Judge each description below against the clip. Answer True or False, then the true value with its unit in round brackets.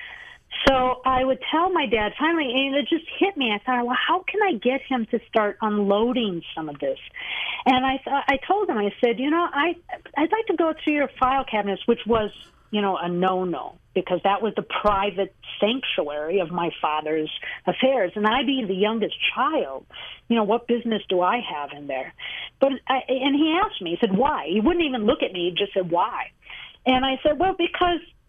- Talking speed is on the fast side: True (210 wpm)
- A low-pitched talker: False (250 Hz)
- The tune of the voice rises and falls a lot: True (6.0 semitones)